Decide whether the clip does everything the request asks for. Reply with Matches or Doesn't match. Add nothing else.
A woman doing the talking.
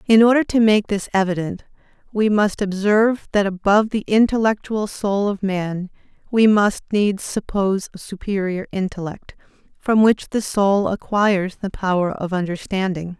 Matches